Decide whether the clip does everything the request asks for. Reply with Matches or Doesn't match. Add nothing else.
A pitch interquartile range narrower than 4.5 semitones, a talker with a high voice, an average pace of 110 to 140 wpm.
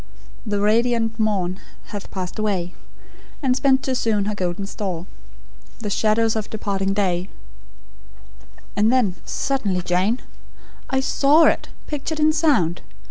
Doesn't match